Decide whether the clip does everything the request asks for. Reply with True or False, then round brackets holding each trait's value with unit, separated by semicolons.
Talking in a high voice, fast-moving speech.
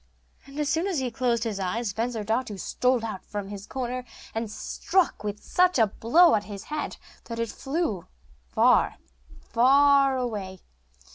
False (235 Hz; 150 wpm)